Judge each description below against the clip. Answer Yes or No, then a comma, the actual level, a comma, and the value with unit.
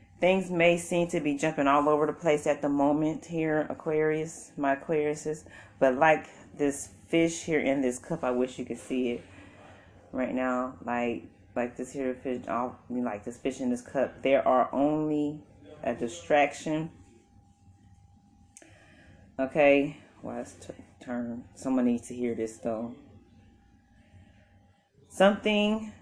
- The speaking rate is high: No, average, 145 wpm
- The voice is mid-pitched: No, low, 130 Hz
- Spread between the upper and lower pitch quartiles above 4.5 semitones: Yes, average, 5.1 semitones